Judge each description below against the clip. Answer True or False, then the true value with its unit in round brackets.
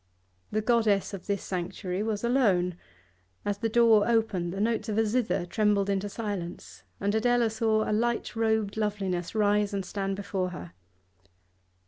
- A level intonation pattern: True (2.3 semitones)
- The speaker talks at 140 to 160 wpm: True (155 wpm)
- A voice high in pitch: True (210 Hz)